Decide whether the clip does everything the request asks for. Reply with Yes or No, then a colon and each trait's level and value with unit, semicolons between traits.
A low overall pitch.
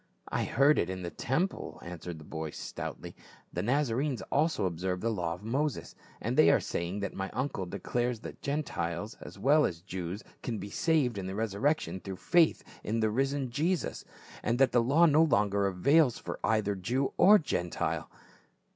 Yes: low, 115 Hz